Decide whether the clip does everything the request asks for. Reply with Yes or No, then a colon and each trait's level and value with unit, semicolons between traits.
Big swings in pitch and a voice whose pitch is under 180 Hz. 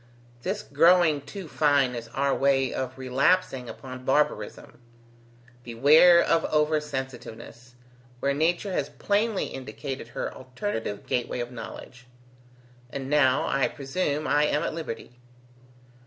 No: average, 3.3 semitones; medium, 140 Hz